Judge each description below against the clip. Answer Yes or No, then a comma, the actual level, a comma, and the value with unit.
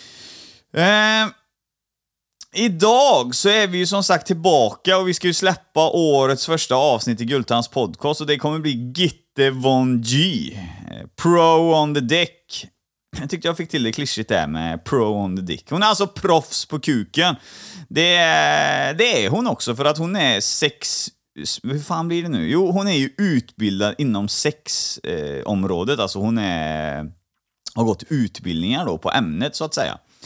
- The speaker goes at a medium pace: Yes, average, 170 wpm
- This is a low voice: No, medium, 150 Hz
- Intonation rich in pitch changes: Yes, wide, 7.0 semitones